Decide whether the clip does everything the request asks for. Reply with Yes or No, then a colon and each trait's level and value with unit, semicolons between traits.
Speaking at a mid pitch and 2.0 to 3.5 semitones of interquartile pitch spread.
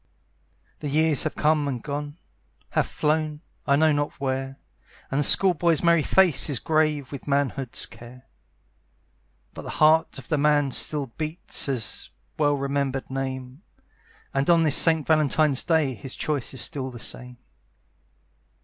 Yes: medium, 145 Hz; narrow, 2.6 semitones